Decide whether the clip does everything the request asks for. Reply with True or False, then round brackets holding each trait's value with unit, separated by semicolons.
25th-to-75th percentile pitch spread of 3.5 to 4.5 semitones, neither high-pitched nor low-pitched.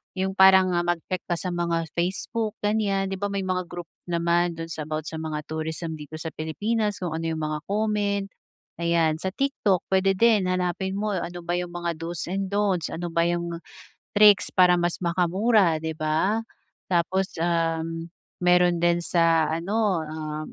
False (2.7 semitones; 175 Hz)